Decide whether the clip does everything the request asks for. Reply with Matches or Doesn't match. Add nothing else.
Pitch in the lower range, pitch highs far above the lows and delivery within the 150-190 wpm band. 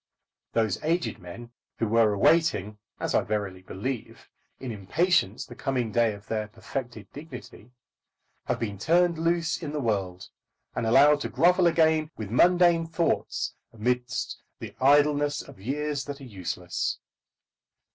Doesn't match